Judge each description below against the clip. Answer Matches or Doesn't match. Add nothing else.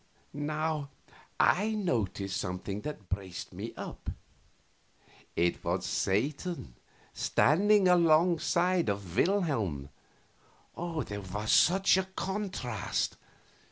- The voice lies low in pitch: Doesn't match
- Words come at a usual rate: Doesn't match